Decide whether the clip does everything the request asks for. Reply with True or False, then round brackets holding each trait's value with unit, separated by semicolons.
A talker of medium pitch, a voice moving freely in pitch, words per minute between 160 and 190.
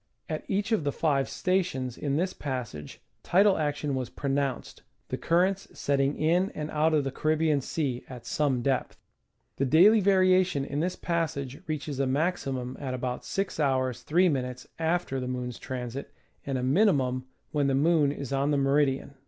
False (145 Hz; 3.9 semitones; 170 wpm)